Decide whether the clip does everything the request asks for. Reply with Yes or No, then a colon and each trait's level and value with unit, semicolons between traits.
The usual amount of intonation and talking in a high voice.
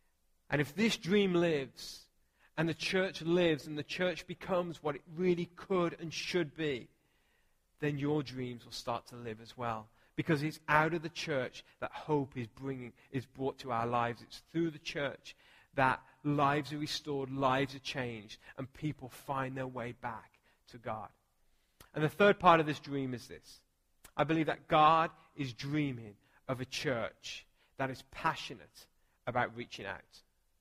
No: average, 4.6 semitones; medium, 140 Hz